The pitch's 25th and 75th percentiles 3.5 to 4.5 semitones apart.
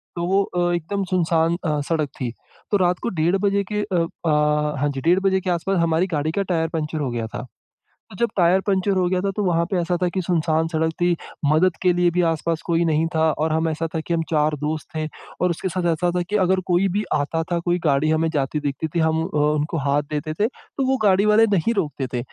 No: average, 2.8 semitones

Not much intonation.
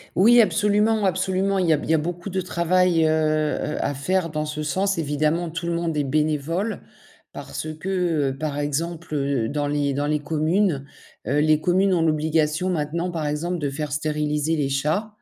No: average, 3.2 semitones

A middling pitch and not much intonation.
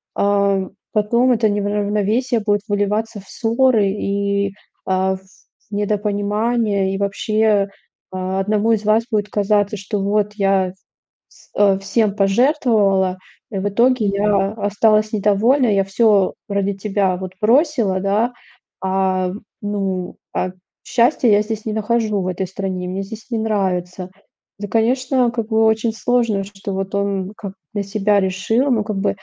No: high, 205 Hz; narrow, 2.2 semitones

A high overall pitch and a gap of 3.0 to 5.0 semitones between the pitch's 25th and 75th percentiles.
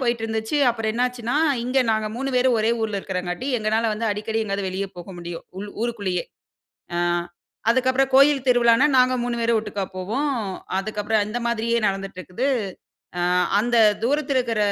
Yes: high, 225 Hz; average, 3.3 semitones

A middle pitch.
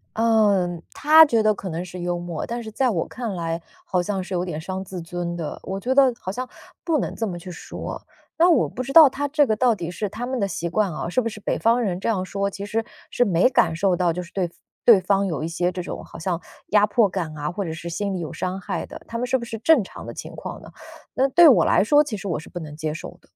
No: high, 195 Hz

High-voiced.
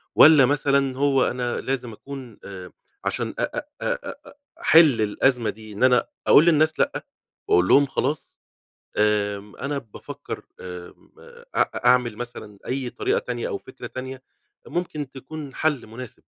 No: low, 130 Hz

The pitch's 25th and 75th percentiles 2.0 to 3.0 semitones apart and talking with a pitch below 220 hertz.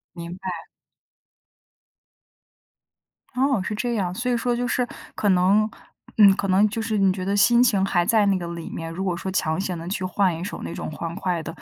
No: average, 3.4 semitones; high, 190 Hz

